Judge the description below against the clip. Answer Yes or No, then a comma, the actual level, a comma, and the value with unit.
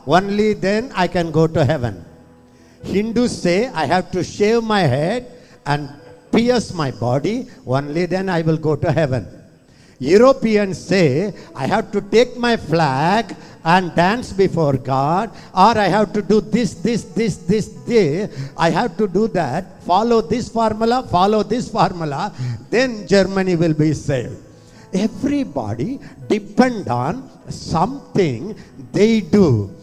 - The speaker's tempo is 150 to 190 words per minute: No, average, 140 wpm